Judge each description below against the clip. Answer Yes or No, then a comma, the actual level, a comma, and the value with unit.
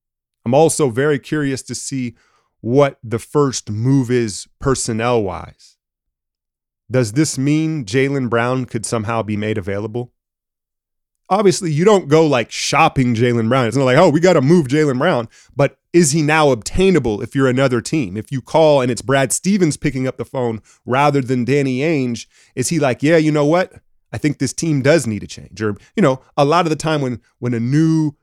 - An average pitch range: Yes, average, 4.5 semitones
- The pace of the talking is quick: No, average, 195 wpm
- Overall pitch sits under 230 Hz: Yes, low, 135 Hz